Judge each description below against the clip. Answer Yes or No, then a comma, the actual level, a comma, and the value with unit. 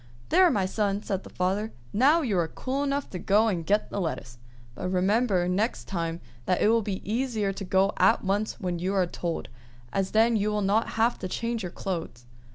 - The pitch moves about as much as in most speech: Yes, average, 3.4 semitones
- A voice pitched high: Yes, high, 200 Hz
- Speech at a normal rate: No, fast, 210 wpm